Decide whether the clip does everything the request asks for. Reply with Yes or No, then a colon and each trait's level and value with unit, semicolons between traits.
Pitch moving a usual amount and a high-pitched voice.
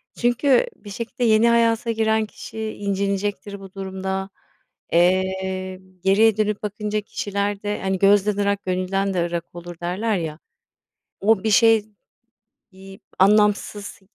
No: narrow, 2.2 semitones; high, 200 Hz